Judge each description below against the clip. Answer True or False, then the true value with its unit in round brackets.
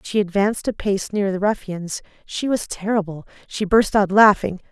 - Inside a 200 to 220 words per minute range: False (180 wpm)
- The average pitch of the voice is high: True (200 Hz)